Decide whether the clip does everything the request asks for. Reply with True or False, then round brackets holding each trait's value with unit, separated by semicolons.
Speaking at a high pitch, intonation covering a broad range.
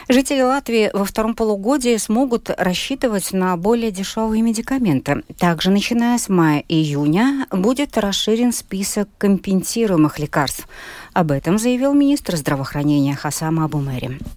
True (200 Hz; 7.0 semitones)